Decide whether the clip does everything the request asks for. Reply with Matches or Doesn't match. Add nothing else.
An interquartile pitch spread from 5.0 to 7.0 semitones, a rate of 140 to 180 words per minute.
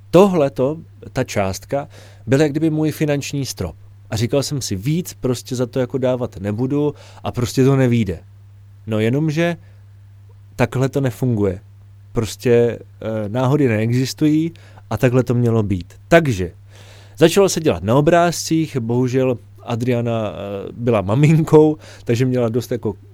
Doesn't match